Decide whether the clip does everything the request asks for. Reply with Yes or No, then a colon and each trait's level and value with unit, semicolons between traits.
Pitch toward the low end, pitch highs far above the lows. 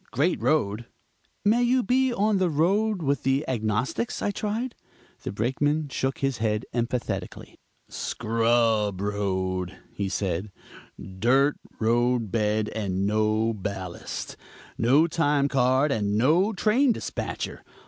Yes: low, 125 Hz; wide, 6.8 semitones